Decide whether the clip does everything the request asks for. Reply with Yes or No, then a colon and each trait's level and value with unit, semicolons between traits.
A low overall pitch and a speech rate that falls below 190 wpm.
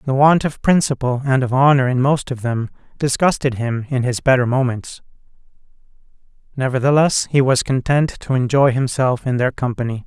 Yes: low, 130 Hz; average, 160 wpm